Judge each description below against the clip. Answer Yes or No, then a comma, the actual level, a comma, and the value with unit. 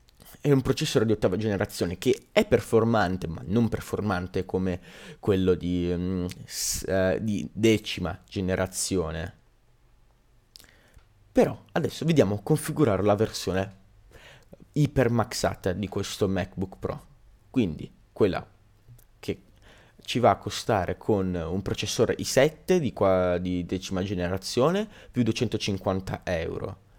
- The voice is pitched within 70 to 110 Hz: Yes, low, 100 Hz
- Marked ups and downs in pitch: No, average, 3.4 semitones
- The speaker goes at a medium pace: No, slow, 110 wpm